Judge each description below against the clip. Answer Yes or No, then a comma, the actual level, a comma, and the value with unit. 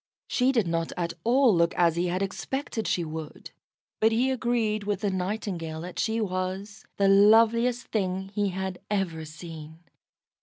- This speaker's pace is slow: No, average, 160 wpm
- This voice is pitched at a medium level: No, high, 195 Hz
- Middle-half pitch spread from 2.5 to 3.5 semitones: No, average, 4.3 semitones